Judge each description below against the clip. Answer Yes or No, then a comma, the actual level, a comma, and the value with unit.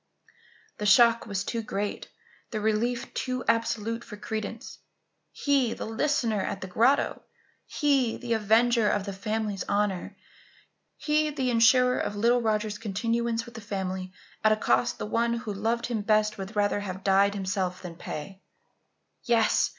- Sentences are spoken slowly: No, average, 155 wpm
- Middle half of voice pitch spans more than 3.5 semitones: No, narrow, 2.6 semitones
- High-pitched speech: Yes, high, 220 Hz